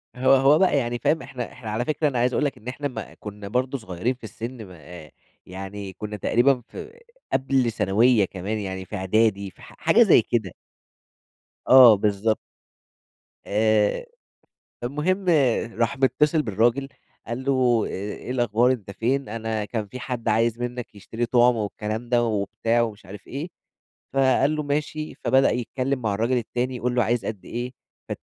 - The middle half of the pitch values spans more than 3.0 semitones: Yes, average, 3.5 semitones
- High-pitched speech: No, low, 120 Hz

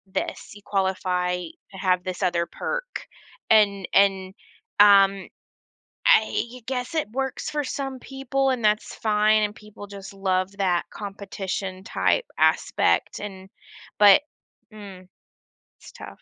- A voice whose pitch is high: Yes, high, 200 Hz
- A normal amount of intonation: Yes, average, 3.8 semitones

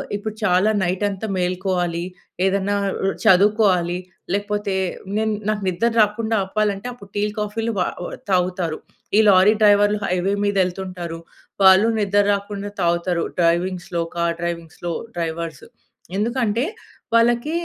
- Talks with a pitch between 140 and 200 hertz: Yes, high, 195 Hz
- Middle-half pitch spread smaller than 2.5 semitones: No, average, 2.9 semitones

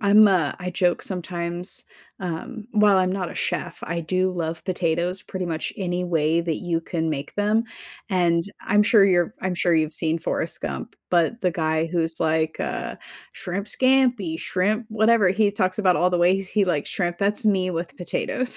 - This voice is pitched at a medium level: Yes, medium, 180 Hz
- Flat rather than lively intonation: No, average, 3.0 semitones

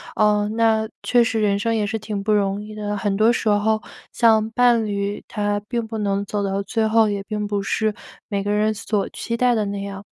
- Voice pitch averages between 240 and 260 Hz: No, high, 210 Hz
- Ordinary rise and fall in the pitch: No, narrow, 1.5 semitones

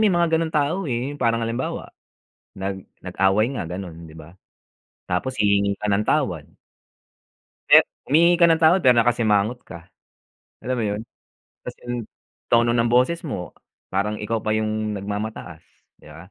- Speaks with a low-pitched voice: Yes, low, 115 Hz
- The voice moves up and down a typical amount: Yes, average, 4.6 semitones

